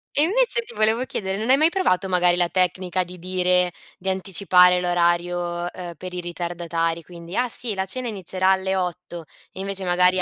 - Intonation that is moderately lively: No, narrow, 1.7 semitones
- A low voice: No, medium, 185 Hz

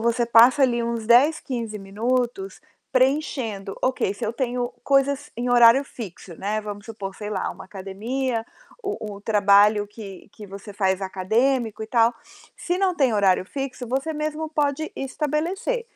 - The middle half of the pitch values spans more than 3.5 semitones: Yes, average, 4.7 semitones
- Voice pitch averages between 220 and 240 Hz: Yes, high, 235 Hz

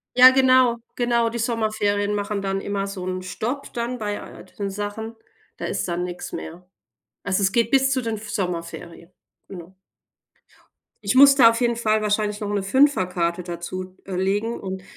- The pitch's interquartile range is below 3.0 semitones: No, average, 4.0 semitones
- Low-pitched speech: No, high, 205 Hz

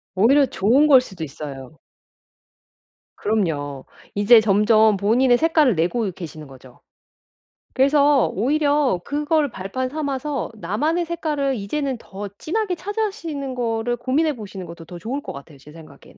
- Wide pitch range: Yes, wide, 7.5 semitones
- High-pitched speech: Yes, high, 240 Hz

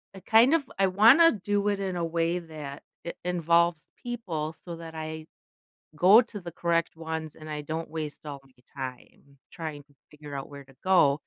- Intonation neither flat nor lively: Yes, average, 3.6 semitones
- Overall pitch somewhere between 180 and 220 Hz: No, medium, 165 Hz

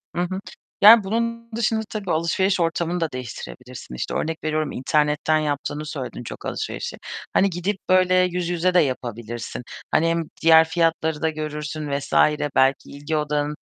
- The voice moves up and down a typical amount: Yes, average, 3.5 semitones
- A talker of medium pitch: Yes, medium, 160 Hz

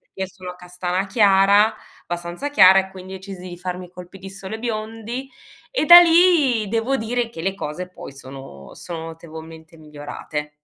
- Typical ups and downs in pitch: Yes, average, 4.3 semitones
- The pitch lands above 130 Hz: Yes, high, 190 Hz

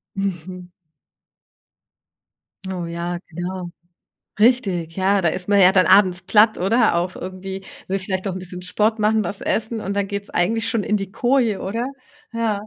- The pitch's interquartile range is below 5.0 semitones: Yes, average, 2.8 semitones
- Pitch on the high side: Yes, high, 195 Hz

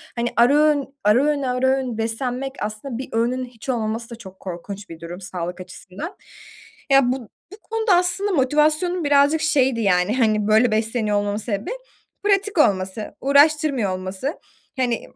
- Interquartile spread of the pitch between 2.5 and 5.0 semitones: No, wide, 5.4 semitones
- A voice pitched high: Yes, high, 245 Hz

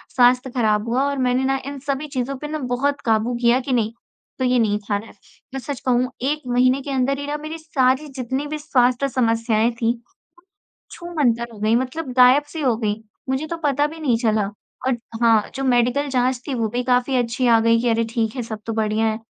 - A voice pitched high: Yes, very high, 250 Hz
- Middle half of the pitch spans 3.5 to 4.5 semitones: No, average, 3.1 semitones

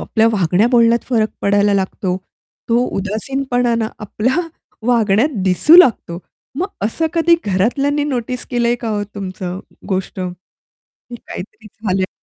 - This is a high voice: Yes, high, 220 Hz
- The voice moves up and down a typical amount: Yes, average, 4.4 semitones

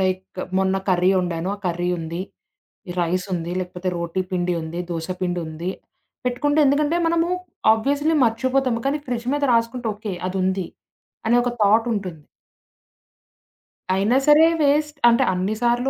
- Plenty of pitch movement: Yes, wide, 5.9 semitones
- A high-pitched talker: Yes, high, 200 Hz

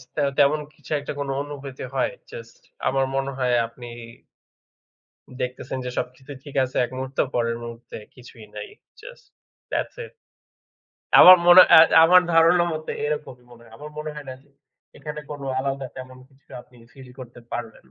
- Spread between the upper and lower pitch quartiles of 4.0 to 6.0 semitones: No, average, 3.1 semitones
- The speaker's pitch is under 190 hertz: Yes, low, 135 Hz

